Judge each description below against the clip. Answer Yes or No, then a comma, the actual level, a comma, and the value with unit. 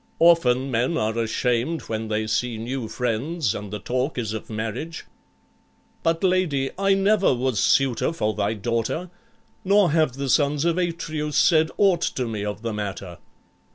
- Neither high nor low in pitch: No, low, 130 Hz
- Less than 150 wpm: No, average, 160 wpm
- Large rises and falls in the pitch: Yes, wide, 6.9 semitones